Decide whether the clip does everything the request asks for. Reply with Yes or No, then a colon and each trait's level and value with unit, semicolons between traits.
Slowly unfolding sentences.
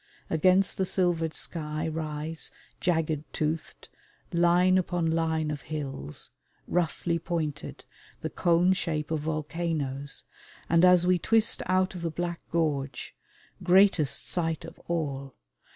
Yes: slow, 120 wpm